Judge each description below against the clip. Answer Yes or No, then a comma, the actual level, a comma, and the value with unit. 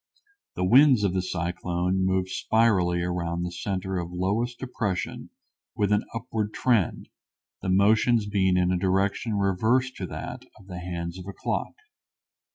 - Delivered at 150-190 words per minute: Yes, average, 155 wpm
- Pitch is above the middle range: No, very low, 95 Hz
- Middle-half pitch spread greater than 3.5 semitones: No, average, 3.1 semitones